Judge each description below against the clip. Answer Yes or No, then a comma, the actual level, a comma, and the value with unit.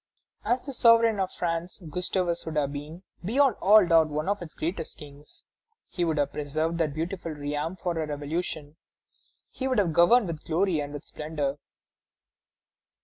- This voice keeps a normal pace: Yes, average, 165 wpm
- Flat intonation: No, average, 3.8 semitones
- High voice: No, medium, 165 Hz